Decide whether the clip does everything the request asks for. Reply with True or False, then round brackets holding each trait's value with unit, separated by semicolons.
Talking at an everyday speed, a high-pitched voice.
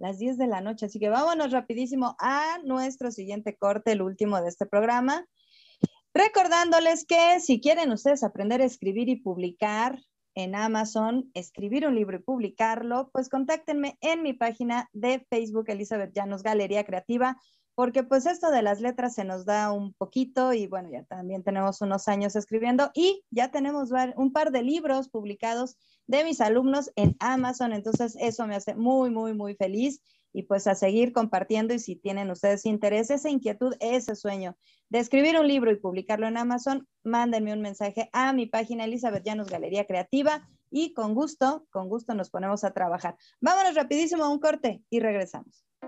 True (175 wpm; 235 Hz)